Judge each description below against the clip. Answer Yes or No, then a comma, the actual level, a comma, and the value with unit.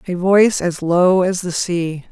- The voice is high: No, medium, 180 Hz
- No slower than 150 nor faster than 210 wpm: Yes, average, 200 wpm